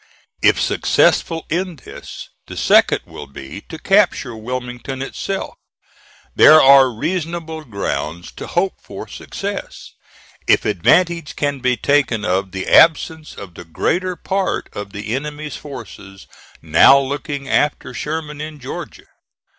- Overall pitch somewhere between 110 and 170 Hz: Yes, medium, 140 Hz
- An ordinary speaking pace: No, slow, 130 wpm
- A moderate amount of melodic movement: No, wide, 6.3 semitones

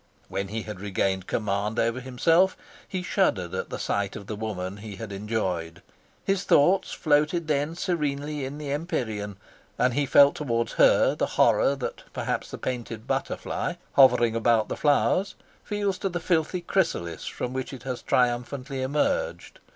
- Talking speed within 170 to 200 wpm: No, average, 160 wpm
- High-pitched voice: No, low, 130 Hz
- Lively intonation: Yes, wide, 6.0 semitones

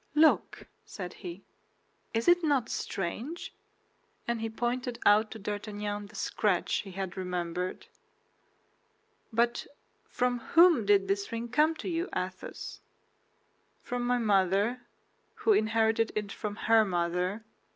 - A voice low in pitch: No, high, 220 Hz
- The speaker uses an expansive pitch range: No, average, 3.9 semitones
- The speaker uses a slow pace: Yes, slow, 125 wpm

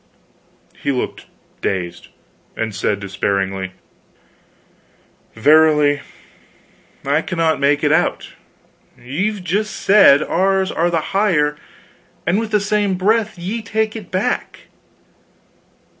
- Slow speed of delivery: Yes, slow, 105 wpm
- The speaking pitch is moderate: Yes, medium, 170 Hz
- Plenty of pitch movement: Yes, wide, 6.3 semitones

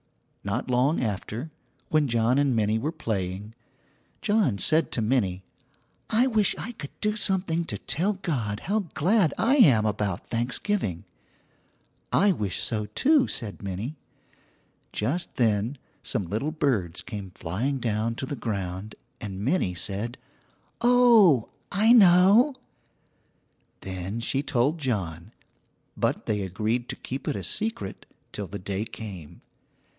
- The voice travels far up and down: Yes, wide, 8.6 semitones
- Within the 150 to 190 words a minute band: No, slow, 135 wpm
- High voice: No, low, 120 Hz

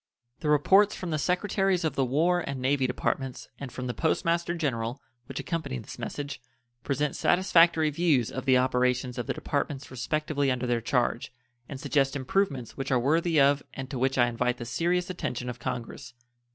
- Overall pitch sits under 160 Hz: Yes, medium, 140 Hz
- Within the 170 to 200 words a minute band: Yes, average, 185 wpm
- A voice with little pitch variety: No, average, 4.2 semitones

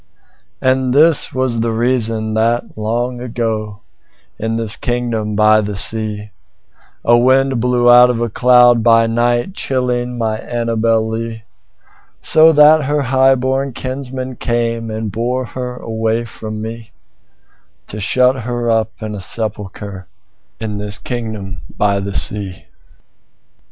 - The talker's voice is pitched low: Yes, low, 115 Hz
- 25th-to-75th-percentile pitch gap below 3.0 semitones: Yes, narrow, 2.4 semitones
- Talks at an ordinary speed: No, slow, 110 wpm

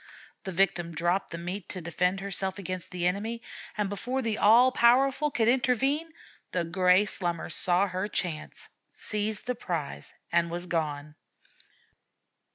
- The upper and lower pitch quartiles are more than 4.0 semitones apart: Yes, average, 4.5 semitones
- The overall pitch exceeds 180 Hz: Yes, high, 190 Hz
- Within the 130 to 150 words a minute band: Yes, average, 145 wpm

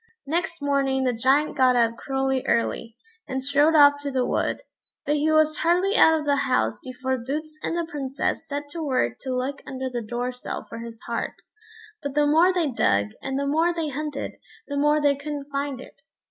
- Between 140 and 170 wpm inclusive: No, average, 200 wpm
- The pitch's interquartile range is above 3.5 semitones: No, average, 2.7 semitones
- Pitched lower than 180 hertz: No, very high, 280 Hz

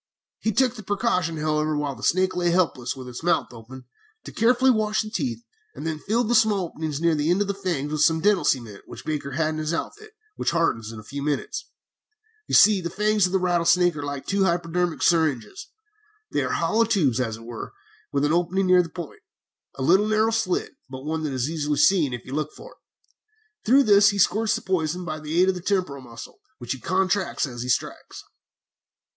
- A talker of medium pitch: Yes, medium, 170 Hz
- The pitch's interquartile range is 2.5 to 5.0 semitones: No, wide, 5.6 semitones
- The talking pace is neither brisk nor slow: No, fast, 220 wpm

